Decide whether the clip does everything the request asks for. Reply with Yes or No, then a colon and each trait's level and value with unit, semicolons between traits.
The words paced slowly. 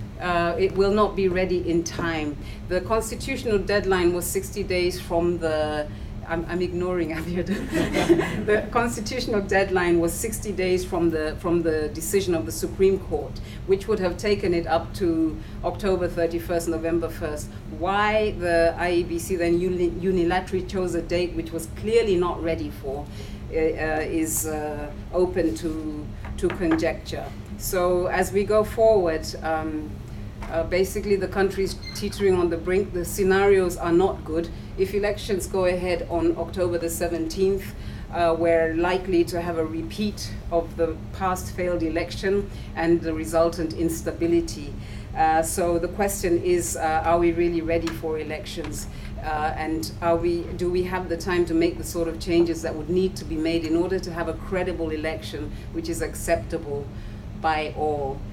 No: average, 160 wpm